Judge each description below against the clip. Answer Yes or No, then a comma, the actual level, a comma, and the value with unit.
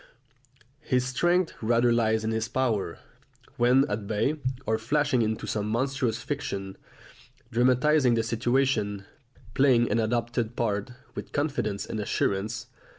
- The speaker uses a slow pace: Yes, slow, 125 wpm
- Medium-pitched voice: No, low, 120 Hz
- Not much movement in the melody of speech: No, average, 3.1 semitones